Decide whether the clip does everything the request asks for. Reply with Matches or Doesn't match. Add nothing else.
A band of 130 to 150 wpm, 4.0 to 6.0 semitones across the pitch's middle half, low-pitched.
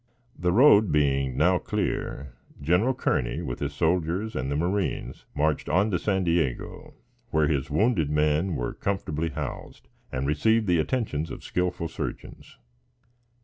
Matches